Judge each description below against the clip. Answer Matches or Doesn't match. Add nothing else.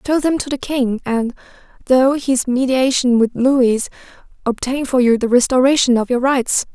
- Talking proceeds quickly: Doesn't match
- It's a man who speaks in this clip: Doesn't match